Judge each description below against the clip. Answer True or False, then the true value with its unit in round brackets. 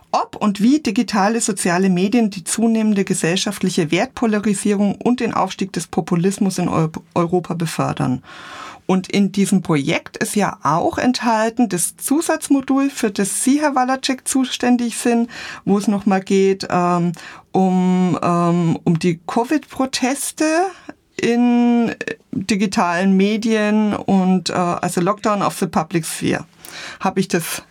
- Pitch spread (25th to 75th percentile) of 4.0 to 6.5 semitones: True (4.5 semitones)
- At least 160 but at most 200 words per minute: False (130 wpm)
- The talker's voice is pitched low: False (205 Hz)